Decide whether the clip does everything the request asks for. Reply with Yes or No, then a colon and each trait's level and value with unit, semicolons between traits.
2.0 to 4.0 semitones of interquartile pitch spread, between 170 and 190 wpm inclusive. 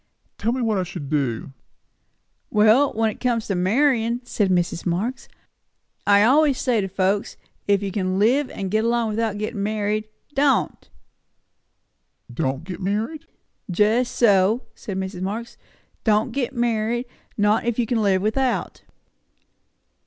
No: average, 3.7 semitones; average, 145 wpm